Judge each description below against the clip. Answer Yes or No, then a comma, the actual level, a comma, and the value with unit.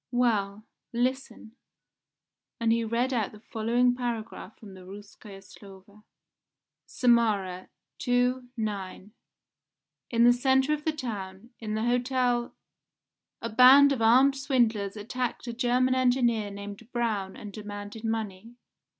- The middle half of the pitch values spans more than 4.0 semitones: No, average, 3.2 semitones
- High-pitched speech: Yes, high, 230 Hz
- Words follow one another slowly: Yes, slow, 125 wpm